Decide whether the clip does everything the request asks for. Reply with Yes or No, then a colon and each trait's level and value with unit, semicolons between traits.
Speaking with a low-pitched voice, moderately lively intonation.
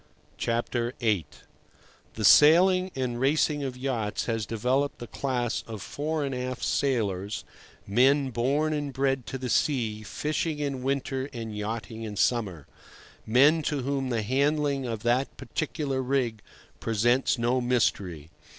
Yes: low, 125 Hz; average, 3.5 semitones